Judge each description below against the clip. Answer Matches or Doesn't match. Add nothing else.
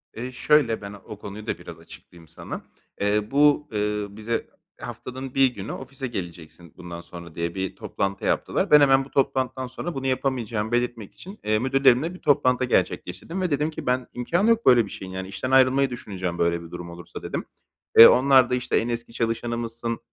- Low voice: Matches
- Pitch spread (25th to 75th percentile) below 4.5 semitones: Doesn't match